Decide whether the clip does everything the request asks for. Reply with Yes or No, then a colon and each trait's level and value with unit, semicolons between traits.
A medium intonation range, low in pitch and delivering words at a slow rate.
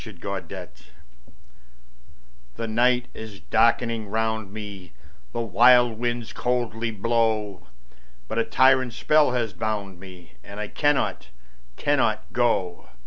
Yes: average, 3.1 semitones; low, 110 Hz; slow, 125 wpm